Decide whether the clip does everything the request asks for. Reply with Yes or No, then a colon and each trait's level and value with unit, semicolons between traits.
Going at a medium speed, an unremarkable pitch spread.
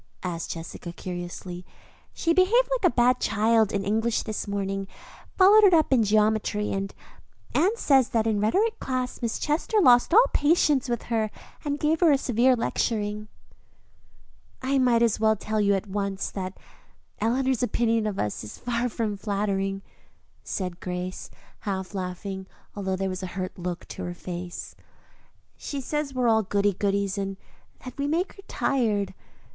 Yes: average, 165 wpm; average, 4.9 semitones